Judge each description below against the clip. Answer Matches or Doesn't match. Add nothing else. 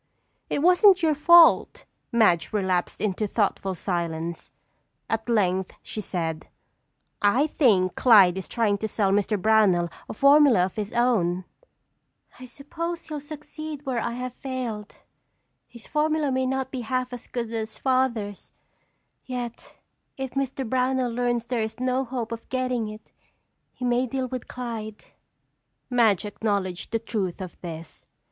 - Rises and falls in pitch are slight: Doesn't match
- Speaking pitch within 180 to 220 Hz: Doesn't match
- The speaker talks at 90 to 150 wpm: Matches